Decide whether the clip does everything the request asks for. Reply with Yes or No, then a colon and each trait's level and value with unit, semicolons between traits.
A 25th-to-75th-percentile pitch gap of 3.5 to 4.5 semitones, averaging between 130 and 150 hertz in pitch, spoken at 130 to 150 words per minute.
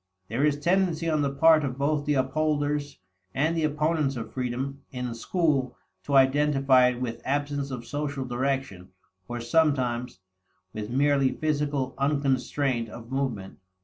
No: average, 2.8 semitones; medium, 140 Hz; average, 145 wpm